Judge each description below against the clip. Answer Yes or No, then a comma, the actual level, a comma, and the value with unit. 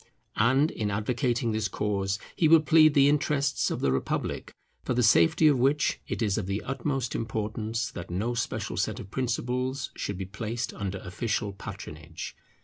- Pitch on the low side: Yes, low, 115 Hz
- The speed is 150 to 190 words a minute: Yes, average, 170 wpm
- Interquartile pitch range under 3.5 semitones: No, average, 5.1 semitones